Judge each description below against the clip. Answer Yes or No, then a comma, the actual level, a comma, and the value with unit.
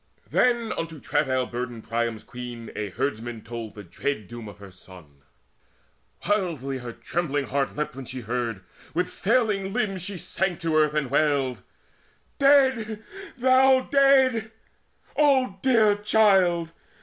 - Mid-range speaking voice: Yes, medium, 155 Hz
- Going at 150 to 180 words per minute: No, slow, 135 wpm